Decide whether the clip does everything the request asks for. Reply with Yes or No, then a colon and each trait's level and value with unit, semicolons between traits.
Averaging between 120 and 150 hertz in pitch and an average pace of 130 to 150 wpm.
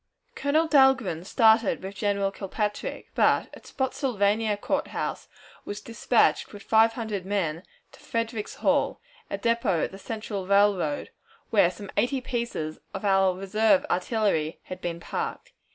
No: high, 205 Hz; slow, 135 wpm